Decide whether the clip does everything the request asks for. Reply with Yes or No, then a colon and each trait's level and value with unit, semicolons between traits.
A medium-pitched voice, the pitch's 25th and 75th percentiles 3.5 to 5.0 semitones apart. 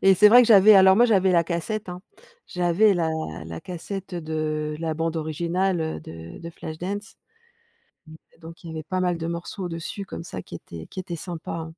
No: medium, 170 Hz; average, 3.1 semitones